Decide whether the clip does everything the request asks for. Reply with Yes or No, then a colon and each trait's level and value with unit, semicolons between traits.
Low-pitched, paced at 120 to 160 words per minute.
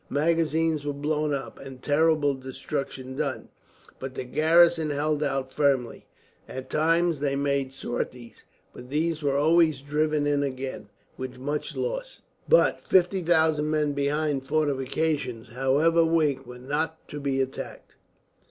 No: medium, 145 Hz; slow, 135 wpm